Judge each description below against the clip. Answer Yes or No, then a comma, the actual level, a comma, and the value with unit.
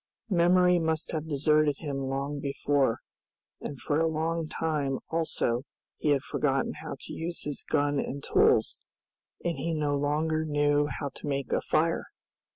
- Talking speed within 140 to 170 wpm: Yes, average, 160 wpm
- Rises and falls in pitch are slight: Yes, narrow, 2.3 semitones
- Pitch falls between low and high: Yes, medium, 150 Hz